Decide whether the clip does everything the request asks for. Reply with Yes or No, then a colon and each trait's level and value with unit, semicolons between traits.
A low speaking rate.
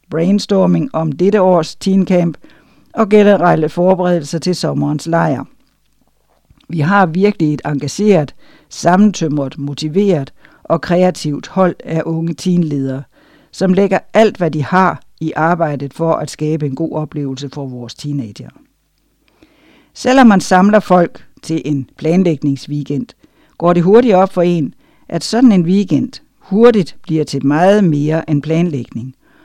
Yes: slow, 130 wpm